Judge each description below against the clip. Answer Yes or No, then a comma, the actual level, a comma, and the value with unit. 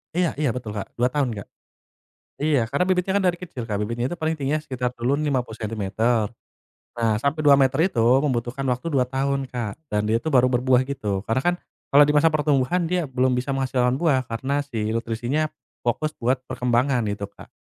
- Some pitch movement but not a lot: Yes, average, 3.8 semitones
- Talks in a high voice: No, low, 130 Hz